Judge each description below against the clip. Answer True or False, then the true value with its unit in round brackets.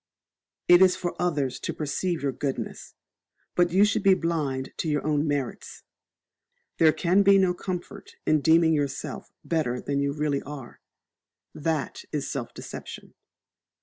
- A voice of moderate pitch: True (155 Hz)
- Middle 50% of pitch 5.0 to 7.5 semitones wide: False (3.8 semitones)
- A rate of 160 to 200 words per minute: False (150 wpm)